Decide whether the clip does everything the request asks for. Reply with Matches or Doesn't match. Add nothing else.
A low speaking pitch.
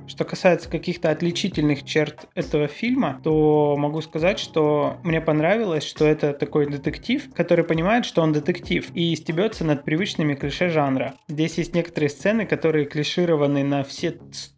Doesn't match